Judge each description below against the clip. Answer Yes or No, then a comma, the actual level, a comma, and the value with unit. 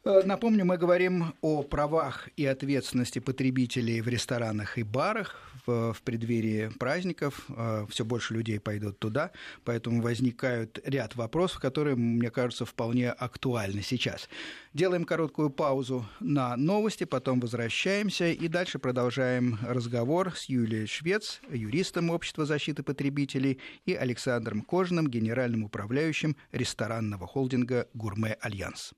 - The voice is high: No, low, 130 Hz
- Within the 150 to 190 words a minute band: No, average, 120 wpm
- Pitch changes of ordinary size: Yes, average, 4.6 semitones